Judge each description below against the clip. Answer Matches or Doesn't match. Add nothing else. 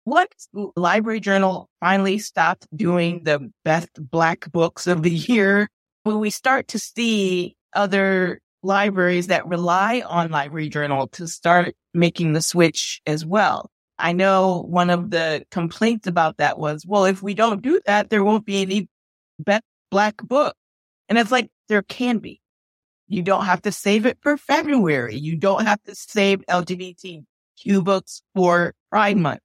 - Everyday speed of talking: Matches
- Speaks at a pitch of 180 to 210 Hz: Matches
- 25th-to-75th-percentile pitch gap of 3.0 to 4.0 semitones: Matches